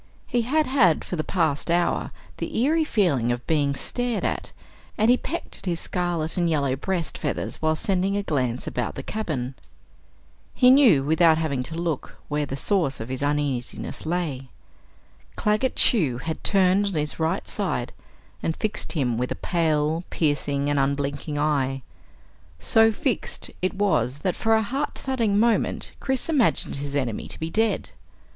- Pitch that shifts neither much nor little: No, wide, 6.5 semitones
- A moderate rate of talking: Yes, average, 165 wpm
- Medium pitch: Yes, medium, 165 Hz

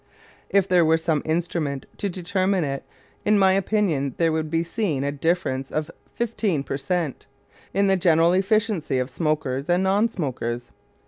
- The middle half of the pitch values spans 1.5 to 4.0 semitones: No, average, 5.0 semitones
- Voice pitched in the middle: Yes, medium, 170 Hz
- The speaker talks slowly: No, average, 165 wpm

